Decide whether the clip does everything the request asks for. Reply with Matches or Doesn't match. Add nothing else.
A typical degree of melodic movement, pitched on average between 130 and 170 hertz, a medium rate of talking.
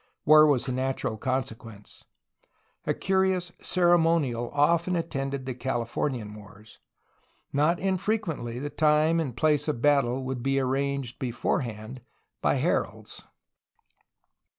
Doesn't match